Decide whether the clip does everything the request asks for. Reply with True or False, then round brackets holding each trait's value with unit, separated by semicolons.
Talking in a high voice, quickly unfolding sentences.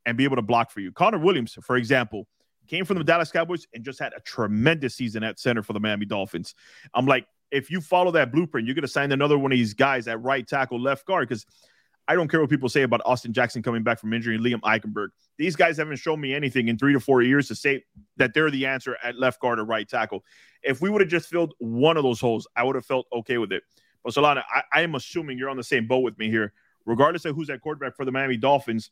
False (130 Hz; 265 wpm)